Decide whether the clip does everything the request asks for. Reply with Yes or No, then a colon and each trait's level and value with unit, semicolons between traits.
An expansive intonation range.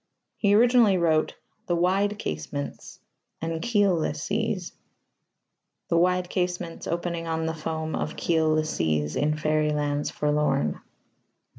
No: average, 3.1 semitones